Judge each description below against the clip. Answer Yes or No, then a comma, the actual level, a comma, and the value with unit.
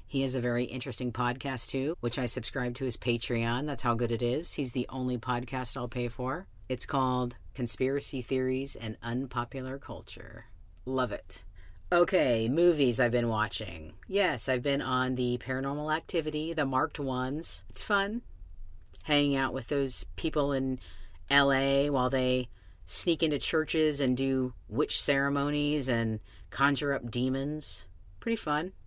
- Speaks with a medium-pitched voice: No, low, 130 Hz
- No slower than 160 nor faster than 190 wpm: No, average, 150 wpm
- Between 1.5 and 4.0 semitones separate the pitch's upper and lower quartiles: Yes, average, 3.0 semitones